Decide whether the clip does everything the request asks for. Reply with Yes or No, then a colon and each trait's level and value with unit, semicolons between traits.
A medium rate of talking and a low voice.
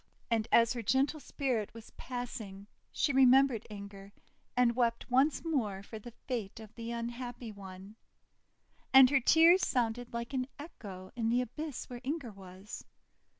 No: average, 150 wpm; high, 235 Hz